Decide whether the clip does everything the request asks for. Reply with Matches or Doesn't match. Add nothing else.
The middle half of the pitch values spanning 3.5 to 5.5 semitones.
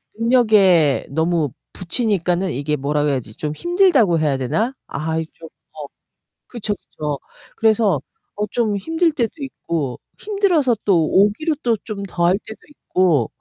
Doesn't match